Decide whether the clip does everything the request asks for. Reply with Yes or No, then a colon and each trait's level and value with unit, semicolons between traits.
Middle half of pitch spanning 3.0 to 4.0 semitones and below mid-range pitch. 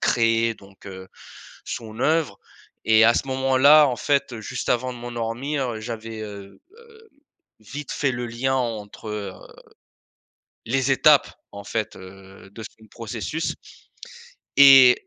Yes: average, 3.7 semitones; low, 115 Hz